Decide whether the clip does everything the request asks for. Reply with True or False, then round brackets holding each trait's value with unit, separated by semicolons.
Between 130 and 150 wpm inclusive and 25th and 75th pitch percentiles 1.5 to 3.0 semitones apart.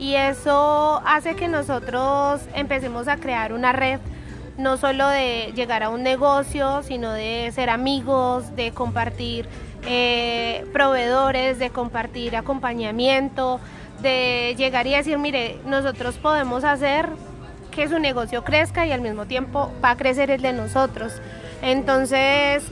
True (135 wpm; 2.4 semitones)